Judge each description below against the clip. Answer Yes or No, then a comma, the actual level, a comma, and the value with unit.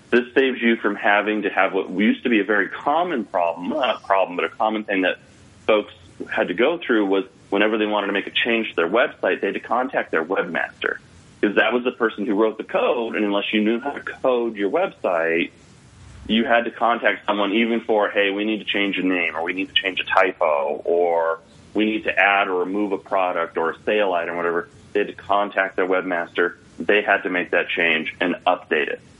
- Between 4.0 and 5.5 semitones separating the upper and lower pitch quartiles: No, average, 3.1 semitones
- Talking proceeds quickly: Yes, fast, 235 wpm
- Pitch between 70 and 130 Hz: Yes, low, 105 Hz